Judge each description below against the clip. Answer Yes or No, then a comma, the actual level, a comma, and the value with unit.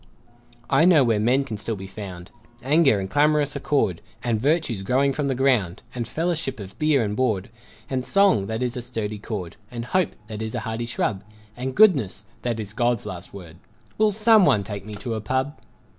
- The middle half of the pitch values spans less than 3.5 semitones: No, average, 5.1 semitones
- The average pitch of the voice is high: No, low, 120 Hz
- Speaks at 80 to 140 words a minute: No, average, 195 wpm